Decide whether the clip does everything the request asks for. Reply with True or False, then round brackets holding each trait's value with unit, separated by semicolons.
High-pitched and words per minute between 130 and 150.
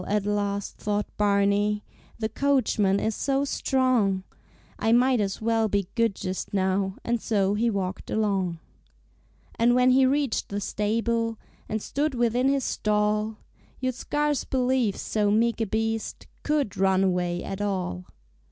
True (215 Hz; 145 wpm)